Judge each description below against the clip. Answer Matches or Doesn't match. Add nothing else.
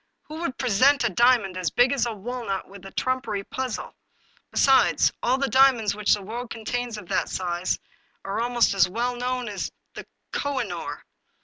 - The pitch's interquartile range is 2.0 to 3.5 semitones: Doesn't match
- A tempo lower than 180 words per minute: Doesn't match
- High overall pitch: Matches